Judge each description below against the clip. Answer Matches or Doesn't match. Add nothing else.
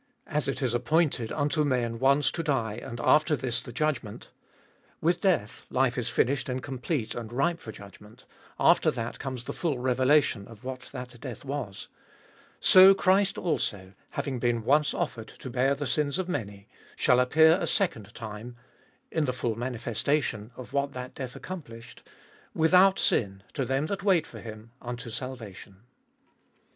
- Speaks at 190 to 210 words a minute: Doesn't match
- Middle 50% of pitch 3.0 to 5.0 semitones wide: Matches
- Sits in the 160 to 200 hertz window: Doesn't match